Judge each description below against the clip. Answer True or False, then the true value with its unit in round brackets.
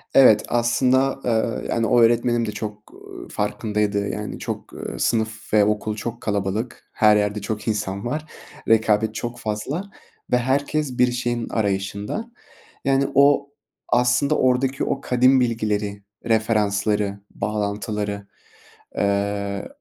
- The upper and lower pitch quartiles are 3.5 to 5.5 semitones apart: False (3.1 semitones)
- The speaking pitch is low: True (110 Hz)